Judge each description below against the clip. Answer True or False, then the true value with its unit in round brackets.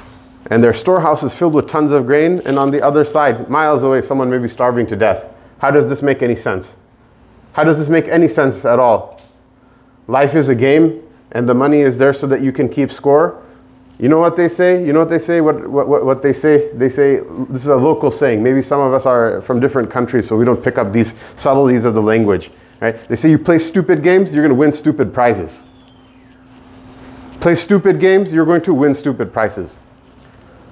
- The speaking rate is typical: False (220 wpm)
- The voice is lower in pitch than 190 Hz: True (135 Hz)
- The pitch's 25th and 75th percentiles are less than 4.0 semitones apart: True (3.6 semitones)